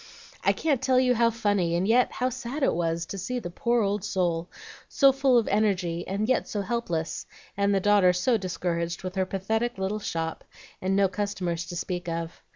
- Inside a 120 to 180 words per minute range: No, average, 200 wpm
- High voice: Yes, high, 195 Hz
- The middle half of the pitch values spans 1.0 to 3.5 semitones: No, average, 4.9 semitones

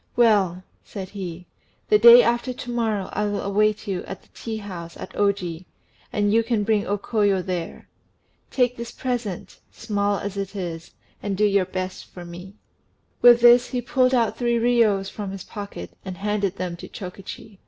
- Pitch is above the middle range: Yes, high, 205 Hz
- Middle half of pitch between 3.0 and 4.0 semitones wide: Yes, average, 3.4 semitones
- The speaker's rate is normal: Yes, average, 180 wpm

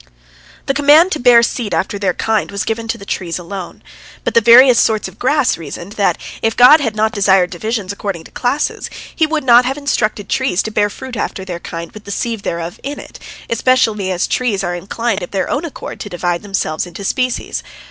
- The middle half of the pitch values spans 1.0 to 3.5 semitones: No, average, 4.8 semitones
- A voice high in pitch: Yes, high, 215 Hz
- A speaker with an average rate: No, fast, 220 wpm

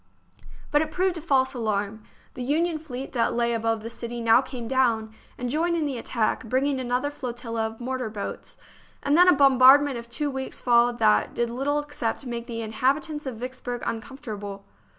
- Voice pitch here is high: Yes, very high, 250 Hz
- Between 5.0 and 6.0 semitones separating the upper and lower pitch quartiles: No, average, 3.5 semitones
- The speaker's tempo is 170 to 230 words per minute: Yes, average, 190 wpm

